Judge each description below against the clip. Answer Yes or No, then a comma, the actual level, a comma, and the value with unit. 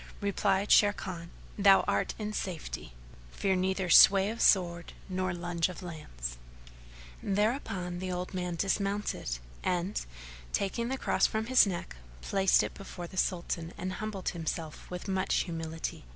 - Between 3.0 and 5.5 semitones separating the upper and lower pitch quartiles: No, narrow, 2.4 semitones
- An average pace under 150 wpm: Yes, average, 140 wpm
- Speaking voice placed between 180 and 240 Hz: Yes, medium, 185 Hz